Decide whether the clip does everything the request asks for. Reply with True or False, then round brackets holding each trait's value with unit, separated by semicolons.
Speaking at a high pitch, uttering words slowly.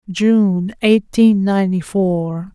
True (195 Hz; 95 wpm)